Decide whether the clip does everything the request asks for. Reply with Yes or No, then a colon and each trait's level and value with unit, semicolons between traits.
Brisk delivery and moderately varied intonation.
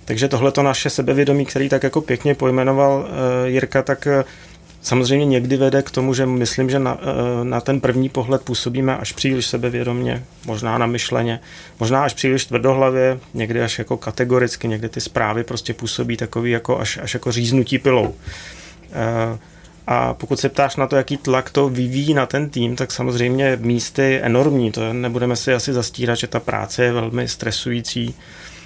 No: fast, 180 wpm; narrow, 2.2 semitones